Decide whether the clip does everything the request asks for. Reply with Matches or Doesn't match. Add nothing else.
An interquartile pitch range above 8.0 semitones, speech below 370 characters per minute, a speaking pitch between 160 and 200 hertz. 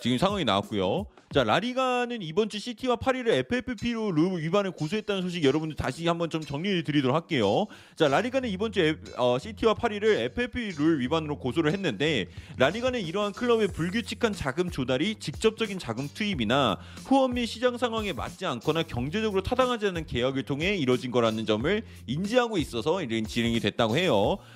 Doesn't match